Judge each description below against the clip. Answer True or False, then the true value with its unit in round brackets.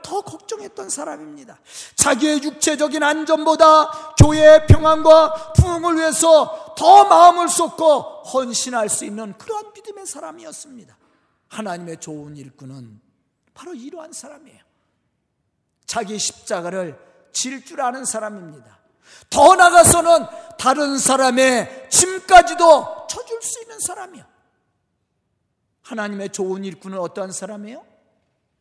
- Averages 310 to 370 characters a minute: False (275 characters per minute)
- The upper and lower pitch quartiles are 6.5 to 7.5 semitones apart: True (7.2 semitones)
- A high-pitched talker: True (305 Hz)